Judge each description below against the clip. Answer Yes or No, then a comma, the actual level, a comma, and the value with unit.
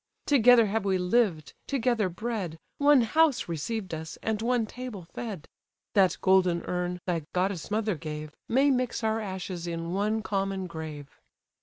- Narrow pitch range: No, average, 4.7 semitones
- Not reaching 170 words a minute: Yes, average, 150 wpm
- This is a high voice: Yes, high, 195 Hz